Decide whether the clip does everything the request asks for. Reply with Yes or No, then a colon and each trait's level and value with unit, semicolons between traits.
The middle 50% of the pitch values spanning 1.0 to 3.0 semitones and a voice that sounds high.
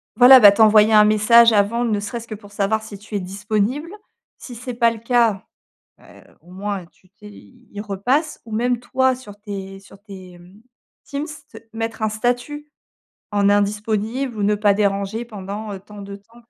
Yes: narrow, 2.6 semitones; high, 215 Hz